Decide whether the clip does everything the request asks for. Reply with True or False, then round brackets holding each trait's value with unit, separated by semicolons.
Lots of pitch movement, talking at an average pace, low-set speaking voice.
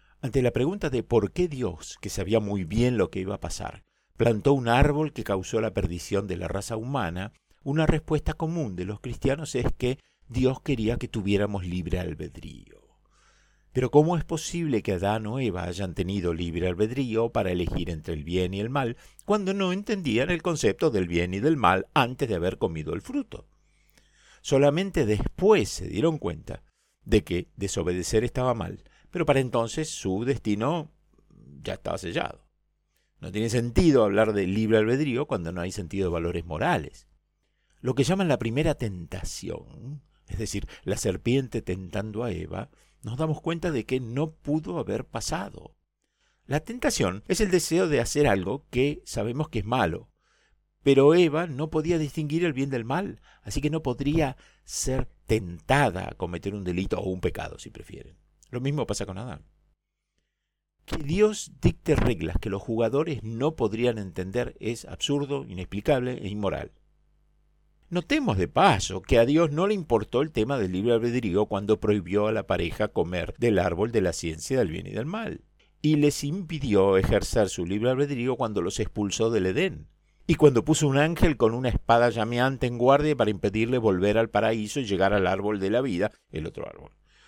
True (7.0 semitones; 175 wpm; 115 Hz)